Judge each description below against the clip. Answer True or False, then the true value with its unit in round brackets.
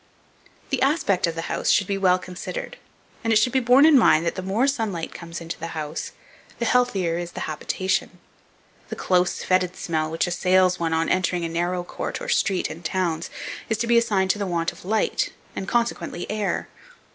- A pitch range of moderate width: True (4.7 semitones)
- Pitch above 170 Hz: True (185 Hz)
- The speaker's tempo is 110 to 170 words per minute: False (205 wpm)